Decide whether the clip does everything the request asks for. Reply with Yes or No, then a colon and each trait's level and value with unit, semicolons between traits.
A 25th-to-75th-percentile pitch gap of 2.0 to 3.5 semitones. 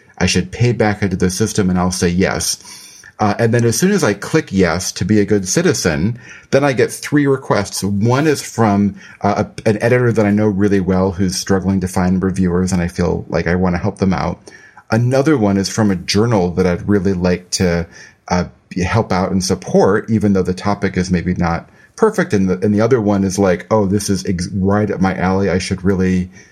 Yes: narrow, 2.6 semitones